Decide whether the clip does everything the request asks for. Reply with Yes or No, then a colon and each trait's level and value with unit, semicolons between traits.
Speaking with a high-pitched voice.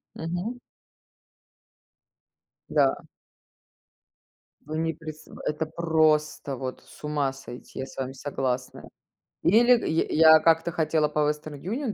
No: medium, 155 Hz